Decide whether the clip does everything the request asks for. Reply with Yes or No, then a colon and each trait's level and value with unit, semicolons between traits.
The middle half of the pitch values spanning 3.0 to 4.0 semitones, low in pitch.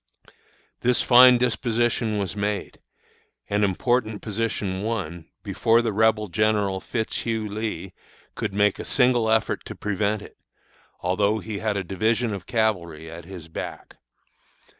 No: narrow, 2.5 semitones; low, 105 Hz